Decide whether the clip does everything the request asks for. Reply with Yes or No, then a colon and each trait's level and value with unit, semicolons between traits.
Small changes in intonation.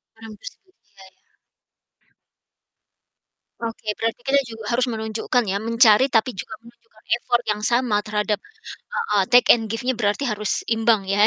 Yes: narrow, 2.2 semitones